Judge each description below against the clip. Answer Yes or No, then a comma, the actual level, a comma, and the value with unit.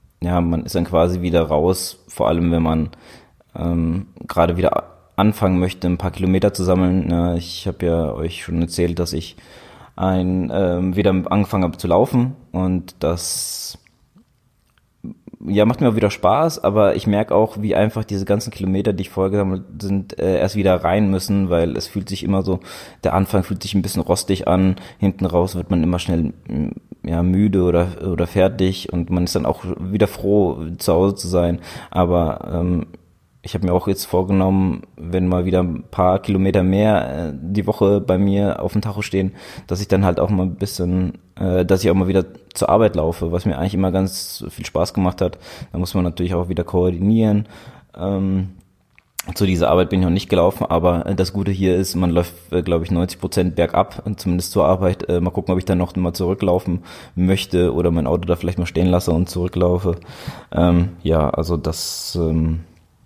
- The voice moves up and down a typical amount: No, narrow, 2.0 semitones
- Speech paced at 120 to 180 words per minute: No, fast, 190 wpm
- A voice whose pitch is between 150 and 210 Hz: No, very low, 90 Hz